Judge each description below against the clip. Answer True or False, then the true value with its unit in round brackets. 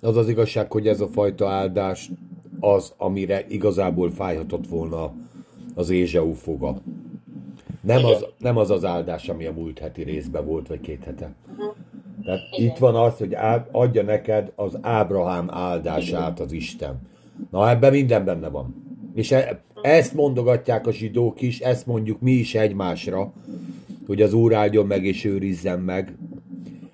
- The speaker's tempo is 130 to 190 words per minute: True (150 wpm)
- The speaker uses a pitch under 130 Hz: True (105 Hz)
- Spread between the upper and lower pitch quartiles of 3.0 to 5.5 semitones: True (4.6 semitones)